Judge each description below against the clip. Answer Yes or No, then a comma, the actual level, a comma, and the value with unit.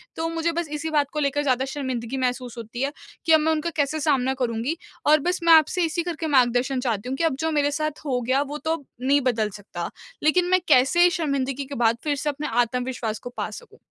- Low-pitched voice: No, very high, 280 Hz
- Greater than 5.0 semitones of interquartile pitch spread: No, average, 3.8 semitones